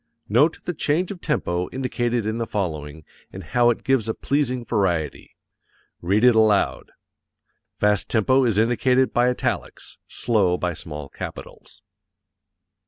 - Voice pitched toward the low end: Yes, low, 115 Hz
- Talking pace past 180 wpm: No, slow, 135 wpm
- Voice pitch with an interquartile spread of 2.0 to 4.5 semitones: No, average, 4.9 semitones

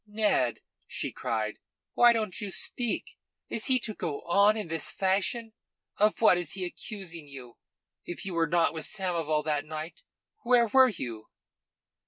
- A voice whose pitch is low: No, medium, 180 Hz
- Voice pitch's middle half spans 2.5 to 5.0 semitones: No, wide, 5.5 semitones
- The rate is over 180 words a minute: No, average, 160 wpm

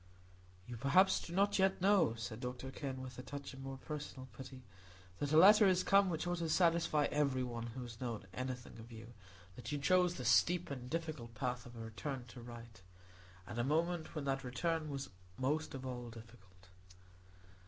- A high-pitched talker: No, low, 135 Hz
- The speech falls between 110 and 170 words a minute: No, average, 195 wpm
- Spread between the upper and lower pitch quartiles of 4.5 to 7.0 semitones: Yes, average, 5.0 semitones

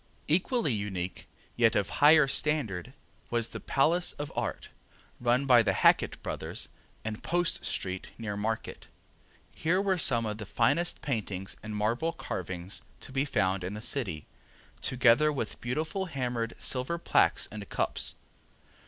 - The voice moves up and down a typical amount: No, wide, 6.1 semitones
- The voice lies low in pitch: Yes, low, 120 Hz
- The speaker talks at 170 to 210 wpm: No, average, 145 wpm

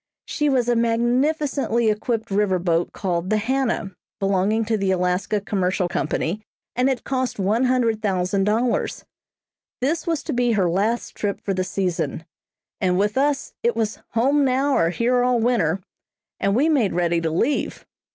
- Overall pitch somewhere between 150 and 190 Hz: No, high, 220 Hz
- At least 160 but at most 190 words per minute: Yes, average, 165 wpm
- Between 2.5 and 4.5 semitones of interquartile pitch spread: No, average, 5.0 semitones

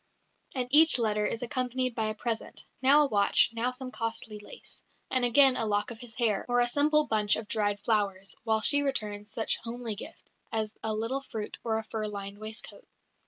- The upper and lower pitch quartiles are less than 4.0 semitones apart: Yes, average, 3.0 semitones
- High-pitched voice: Yes, high, 225 Hz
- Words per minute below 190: No, fast, 205 wpm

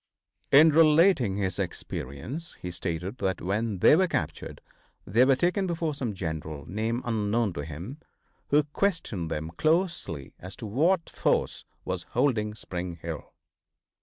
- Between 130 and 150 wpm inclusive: Yes, average, 140 wpm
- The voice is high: No, low, 110 Hz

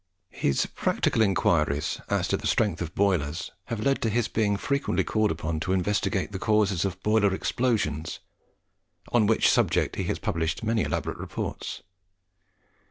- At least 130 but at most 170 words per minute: Yes, average, 155 wpm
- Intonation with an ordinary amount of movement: Yes, average, 4.7 semitones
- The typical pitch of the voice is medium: No, low, 100 Hz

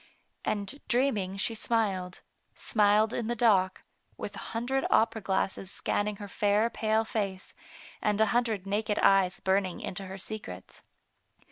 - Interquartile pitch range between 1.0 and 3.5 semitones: Yes, narrow, 2.5 semitones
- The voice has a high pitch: Yes, high, 205 Hz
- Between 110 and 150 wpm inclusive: Yes, average, 140 wpm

